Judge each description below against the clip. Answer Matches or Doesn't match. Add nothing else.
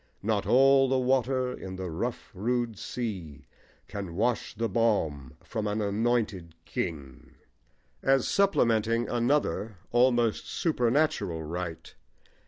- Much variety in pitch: Doesn't match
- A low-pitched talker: Matches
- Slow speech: Matches